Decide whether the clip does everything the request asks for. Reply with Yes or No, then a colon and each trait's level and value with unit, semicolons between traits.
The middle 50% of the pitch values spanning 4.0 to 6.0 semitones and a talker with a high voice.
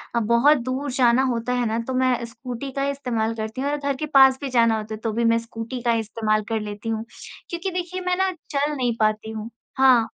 No: average, 3.4 semitones; high, 240 Hz